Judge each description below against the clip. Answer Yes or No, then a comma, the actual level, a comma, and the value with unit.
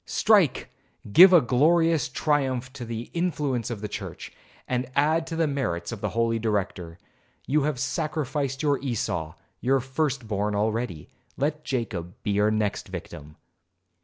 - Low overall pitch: Yes, low, 125 Hz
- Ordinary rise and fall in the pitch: No, wide, 5.8 semitones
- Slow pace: No, average, 150 wpm